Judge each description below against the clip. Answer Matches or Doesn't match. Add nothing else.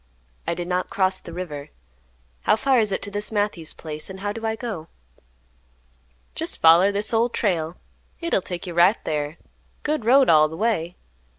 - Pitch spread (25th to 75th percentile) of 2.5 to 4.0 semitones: Doesn't match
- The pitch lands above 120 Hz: Matches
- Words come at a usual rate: Matches